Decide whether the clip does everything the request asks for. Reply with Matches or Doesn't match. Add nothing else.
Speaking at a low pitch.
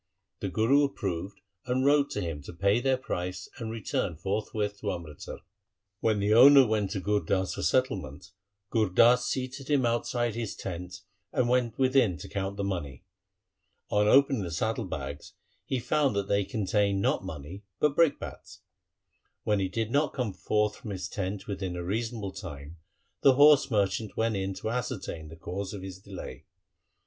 Matches